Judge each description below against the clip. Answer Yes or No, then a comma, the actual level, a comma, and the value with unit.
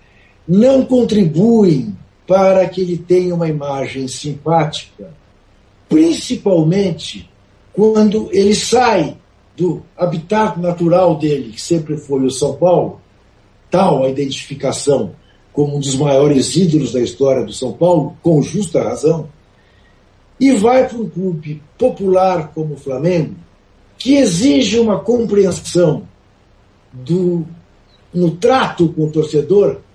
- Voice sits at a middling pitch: Yes, medium, 165 Hz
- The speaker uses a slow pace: Yes, slow, 115 wpm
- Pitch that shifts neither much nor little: No, wide, 5.8 semitones